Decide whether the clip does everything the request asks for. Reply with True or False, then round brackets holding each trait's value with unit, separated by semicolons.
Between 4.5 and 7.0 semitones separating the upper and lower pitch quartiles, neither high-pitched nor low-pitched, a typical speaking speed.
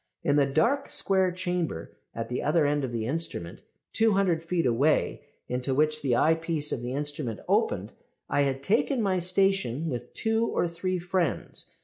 True (5.3 semitones; 160 Hz; 165 wpm)